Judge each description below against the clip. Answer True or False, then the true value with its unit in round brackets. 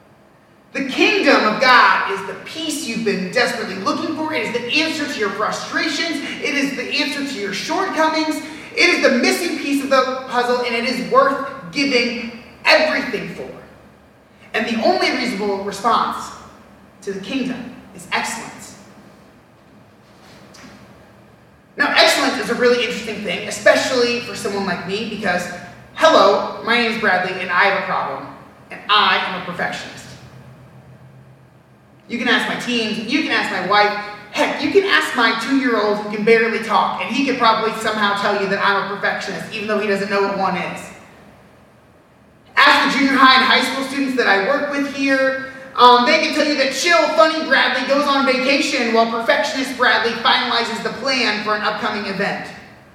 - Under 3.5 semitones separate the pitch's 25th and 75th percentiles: False (4.8 semitones)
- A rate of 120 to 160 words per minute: False (175 wpm)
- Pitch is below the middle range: False (245 Hz)